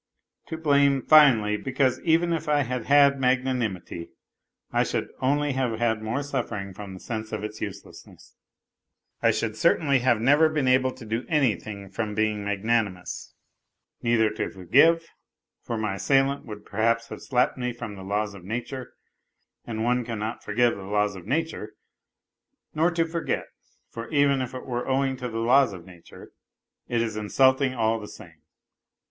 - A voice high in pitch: No, low, 120 Hz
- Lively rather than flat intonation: No, average, 4.2 semitones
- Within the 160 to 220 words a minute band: Yes, average, 170 wpm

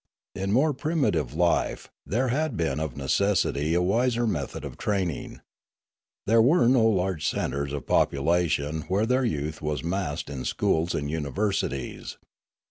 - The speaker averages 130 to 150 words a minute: Yes, average, 140 wpm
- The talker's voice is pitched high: No, very low, 90 Hz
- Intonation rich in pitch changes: Yes, wide, 7.4 semitones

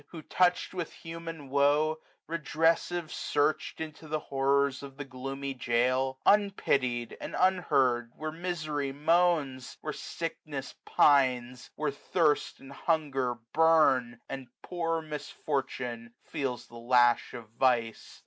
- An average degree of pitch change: Yes, average, 3.9 semitones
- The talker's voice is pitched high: No, medium, 140 Hz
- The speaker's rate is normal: No, slow, 120 wpm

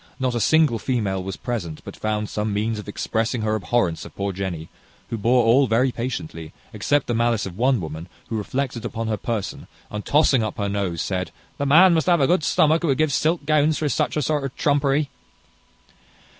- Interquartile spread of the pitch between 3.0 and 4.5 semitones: No, wide, 5.5 semitones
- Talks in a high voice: No, low, 115 Hz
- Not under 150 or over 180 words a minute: No, fast, 205 wpm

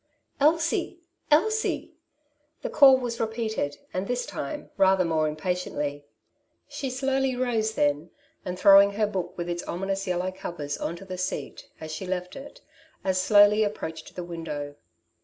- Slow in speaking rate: No, average, 160 wpm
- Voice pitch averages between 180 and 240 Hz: Yes, high, 190 Hz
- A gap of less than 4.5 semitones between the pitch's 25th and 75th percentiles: No, average, 5.0 semitones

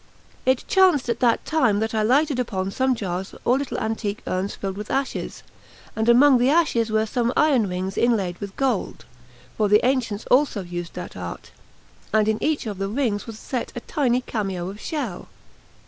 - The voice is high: Yes, high, 225 Hz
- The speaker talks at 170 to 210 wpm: Yes, average, 185 wpm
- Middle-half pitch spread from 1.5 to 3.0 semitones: No, average, 4.4 semitones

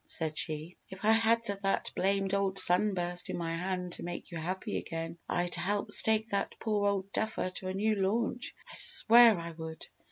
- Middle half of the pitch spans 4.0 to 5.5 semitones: No, average, 3.3 semitones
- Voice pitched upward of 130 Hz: Yes, high, 190 Hz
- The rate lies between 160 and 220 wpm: Yes, average, 190 wpm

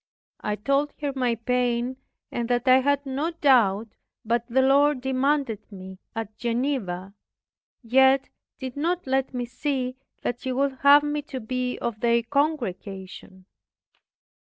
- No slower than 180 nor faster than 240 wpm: No, average, 140 wpm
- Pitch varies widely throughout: No, average, 3.2 semitones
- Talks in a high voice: Yes, very high, 255 Hz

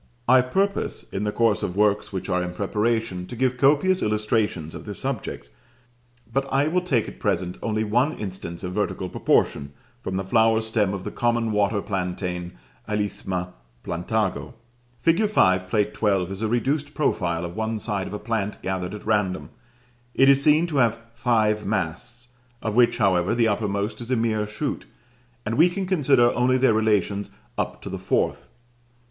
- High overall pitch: No, low, 110 Hz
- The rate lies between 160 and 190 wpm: Yes, average, 175 wpm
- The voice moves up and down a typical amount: Yes, average, 4.1 semitones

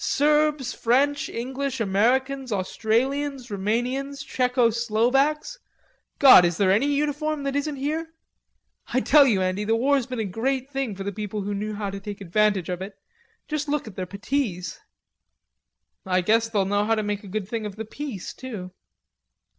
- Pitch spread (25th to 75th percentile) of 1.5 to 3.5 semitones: No, average, 5.3 semitones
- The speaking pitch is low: No, high, 230 Hz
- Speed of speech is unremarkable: Yes, average, 170 wpm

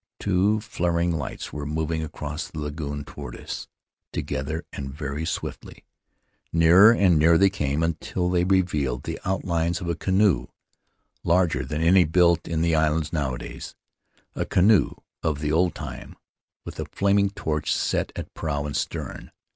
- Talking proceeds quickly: No, average, 165 wpm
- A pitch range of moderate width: Yes, average, 3.1 semitones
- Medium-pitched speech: No, very low, 80 Hz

